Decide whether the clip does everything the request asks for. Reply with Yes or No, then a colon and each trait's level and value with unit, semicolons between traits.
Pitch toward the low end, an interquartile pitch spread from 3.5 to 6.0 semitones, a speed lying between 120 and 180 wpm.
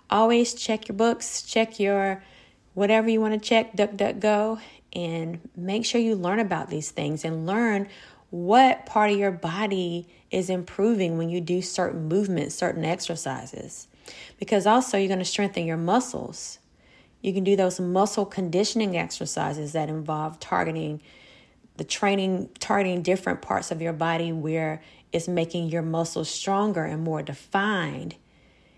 No: medium, 185 Hz; average, 3.9 semitones; average, 150 wpm